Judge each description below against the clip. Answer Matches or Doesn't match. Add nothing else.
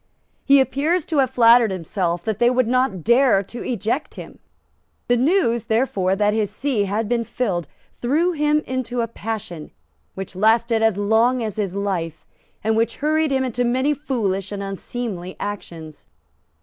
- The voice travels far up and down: Doesn't match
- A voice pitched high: Matches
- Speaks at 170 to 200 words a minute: Doesn't match